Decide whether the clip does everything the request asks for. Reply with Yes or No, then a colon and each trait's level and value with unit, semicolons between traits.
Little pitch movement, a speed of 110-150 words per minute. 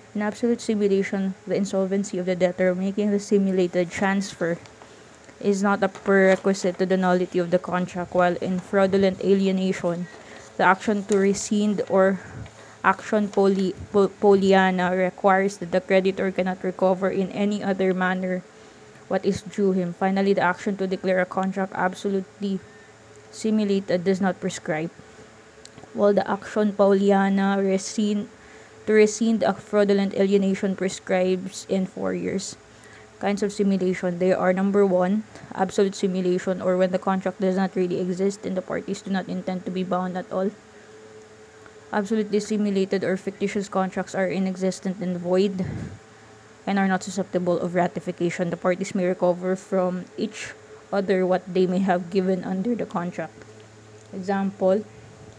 Yes: narrow, 1.6 semitones; average, 145 wpm